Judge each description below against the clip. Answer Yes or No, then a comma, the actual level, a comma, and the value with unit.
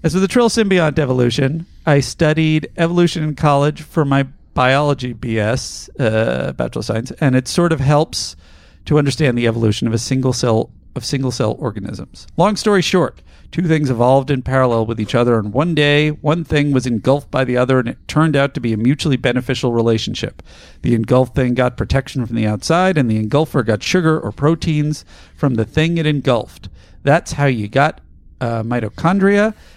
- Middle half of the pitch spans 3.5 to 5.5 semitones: Yes, average, 4.9 semitones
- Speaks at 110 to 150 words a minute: No, average, 185 wpm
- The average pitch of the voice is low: Yes, low, 130 Hz